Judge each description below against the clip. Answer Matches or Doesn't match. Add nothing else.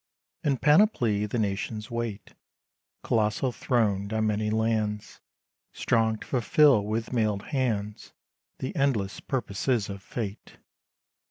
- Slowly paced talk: Matches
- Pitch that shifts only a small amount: Doesn't match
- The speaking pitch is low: Matches